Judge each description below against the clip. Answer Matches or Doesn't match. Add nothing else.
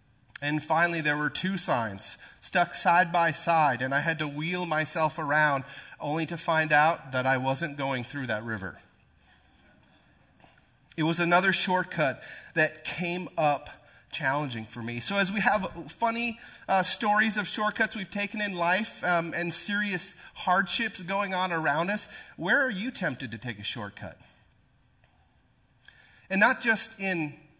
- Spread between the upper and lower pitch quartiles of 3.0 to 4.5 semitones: Doesn't match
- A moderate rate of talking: Matches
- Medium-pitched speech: Matches